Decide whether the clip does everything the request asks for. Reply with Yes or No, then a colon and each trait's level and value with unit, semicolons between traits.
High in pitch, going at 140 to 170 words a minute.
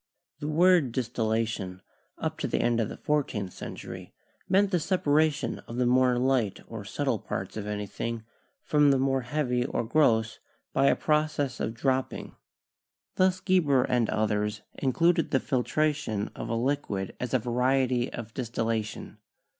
No: low, 125 Hz; average, 155 wpm